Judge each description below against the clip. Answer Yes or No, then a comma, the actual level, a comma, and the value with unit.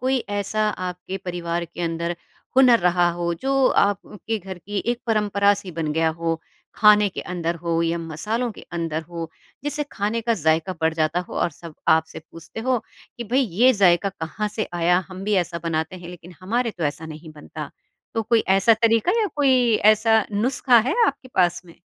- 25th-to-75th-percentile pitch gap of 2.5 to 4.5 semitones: No, average, 4.9 semitones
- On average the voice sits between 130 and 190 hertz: Yes, medium, 185 Hz